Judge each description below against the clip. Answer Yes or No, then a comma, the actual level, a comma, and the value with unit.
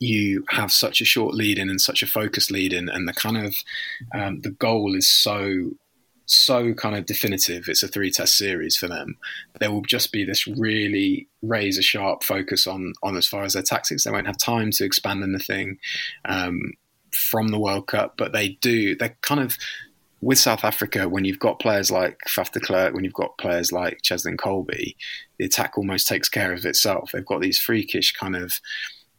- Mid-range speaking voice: No, low, 100 Hz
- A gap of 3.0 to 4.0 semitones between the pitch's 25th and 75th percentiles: No, narrow, 2.6 semitones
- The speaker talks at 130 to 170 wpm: No, average, 200 wpm